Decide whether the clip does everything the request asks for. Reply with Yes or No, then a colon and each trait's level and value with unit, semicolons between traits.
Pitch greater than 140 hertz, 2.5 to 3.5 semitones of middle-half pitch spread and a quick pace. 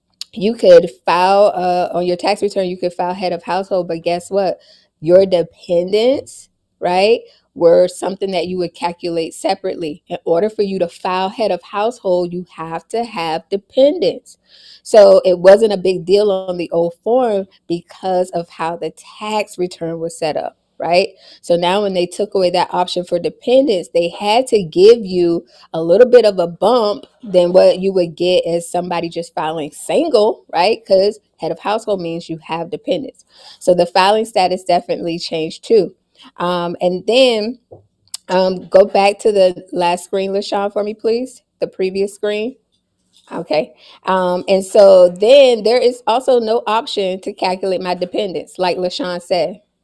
No: medium, 185 Hz; average, 3.2 semitones; average, 170 wpm